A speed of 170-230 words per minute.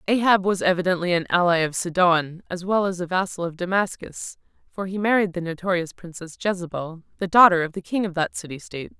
Yes: average, 200 wpm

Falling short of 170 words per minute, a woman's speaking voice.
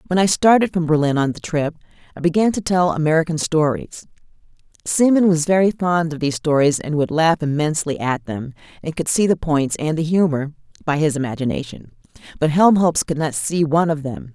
No: average, 190 wpm; female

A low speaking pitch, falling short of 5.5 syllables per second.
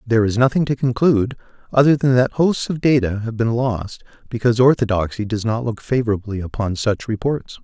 No: low, 120 Hz; 5.7 syllables/s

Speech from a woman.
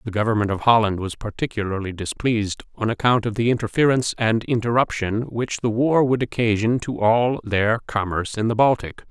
No: male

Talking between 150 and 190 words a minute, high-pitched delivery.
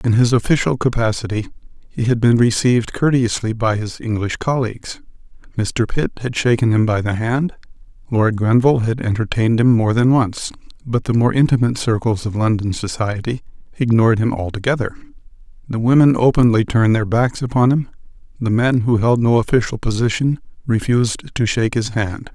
No: average, 160 wpm; low, 115 Hz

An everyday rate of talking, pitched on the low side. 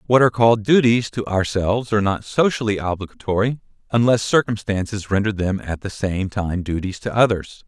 Yes: average, 165 wpm; low, 105 Hz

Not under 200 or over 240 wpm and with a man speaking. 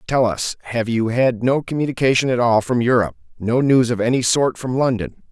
No: average, 190 wpm; male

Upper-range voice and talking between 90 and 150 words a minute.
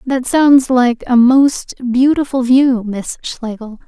Yes: very high, 250 Hz; average, 140 wpm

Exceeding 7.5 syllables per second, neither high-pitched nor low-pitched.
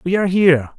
Yes: 8.1 syllables/s; medium, 170 Hz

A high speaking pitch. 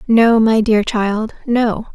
Yes: high, 220 Hz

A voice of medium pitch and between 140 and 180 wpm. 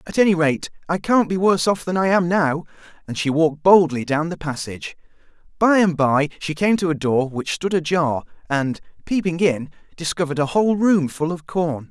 No: medium, 165 Hz; average, 200 wpm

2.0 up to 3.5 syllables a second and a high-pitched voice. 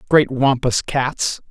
No: 3.2 syllables/s; low, 135 Hz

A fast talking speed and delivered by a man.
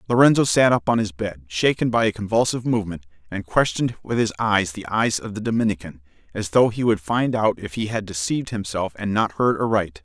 Yes: fast, 215 wpm; male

